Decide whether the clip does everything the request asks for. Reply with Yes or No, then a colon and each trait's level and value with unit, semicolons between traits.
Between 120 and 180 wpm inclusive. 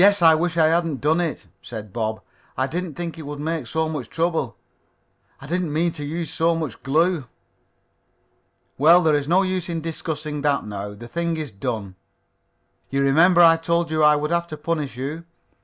No: average, 190 wpm